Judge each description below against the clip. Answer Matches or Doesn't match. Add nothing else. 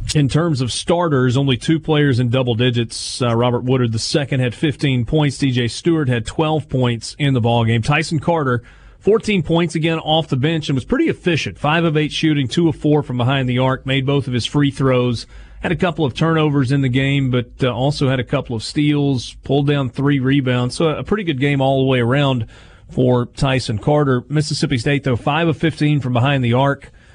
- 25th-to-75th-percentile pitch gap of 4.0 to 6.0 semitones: Doesn't match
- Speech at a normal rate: Doesn't match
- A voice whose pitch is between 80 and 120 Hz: Doesn't match